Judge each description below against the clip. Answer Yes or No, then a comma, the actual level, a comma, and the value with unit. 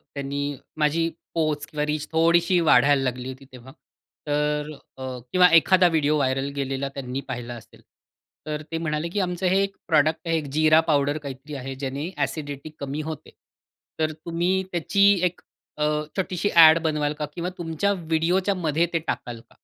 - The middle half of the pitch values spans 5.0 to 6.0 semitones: No, average, 3.0 semitones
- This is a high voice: No, medium, 150 Hz